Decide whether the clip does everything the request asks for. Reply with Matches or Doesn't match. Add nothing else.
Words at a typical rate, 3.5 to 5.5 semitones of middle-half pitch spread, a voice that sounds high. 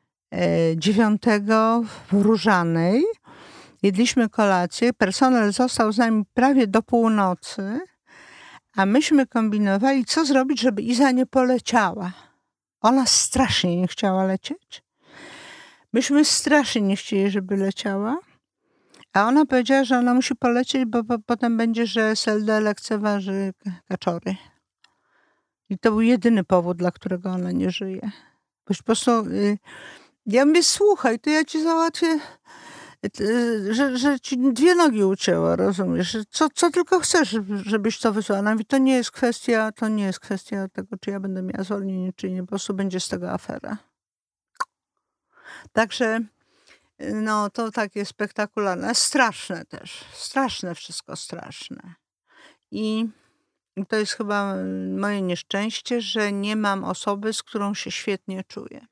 Matches